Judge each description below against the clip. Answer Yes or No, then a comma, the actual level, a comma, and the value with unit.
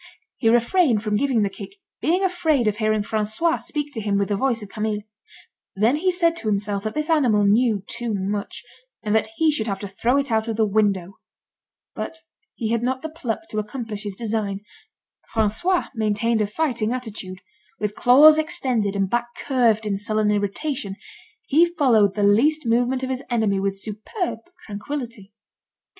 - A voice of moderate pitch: No, high, 225 Hz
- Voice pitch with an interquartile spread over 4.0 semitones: Yes, average, 4.5 semitones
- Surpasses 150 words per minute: Yes, average, 180 wpm